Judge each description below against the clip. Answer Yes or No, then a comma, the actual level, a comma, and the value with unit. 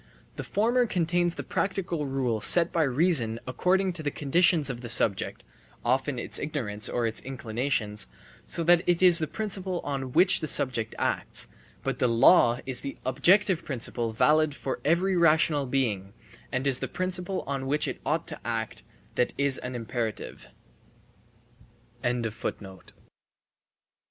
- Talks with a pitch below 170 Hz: Yes, medium, 140 Hz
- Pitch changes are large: Yes, wide, 6.1 semitones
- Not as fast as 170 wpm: Yes, average, 145 wpm